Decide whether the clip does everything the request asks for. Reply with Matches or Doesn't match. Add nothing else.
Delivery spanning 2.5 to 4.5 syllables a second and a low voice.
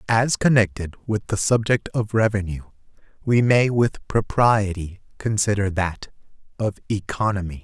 Matches